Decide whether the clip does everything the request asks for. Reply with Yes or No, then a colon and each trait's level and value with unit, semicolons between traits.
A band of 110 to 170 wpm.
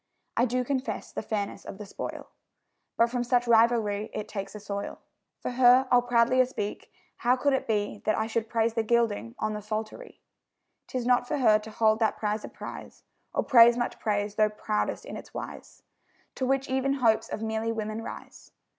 No: average, 195 wpm